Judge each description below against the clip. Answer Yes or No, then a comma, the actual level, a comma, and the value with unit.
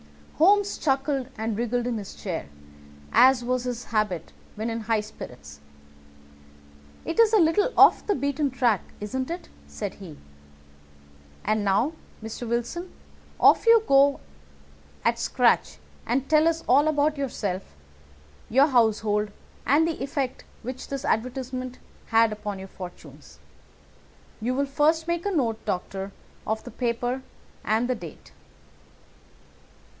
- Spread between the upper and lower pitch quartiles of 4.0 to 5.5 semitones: Yes, average, 4.7 semitones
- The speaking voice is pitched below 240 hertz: No, very high, 250 Hz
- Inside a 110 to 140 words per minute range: Yes, slow, 135 wpm